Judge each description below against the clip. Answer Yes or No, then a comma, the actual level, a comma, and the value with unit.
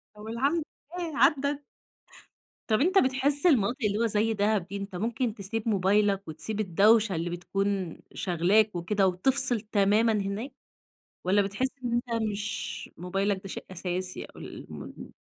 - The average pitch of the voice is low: No, high, 210 Hz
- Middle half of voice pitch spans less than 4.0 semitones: Yes, average, 3.1 semitones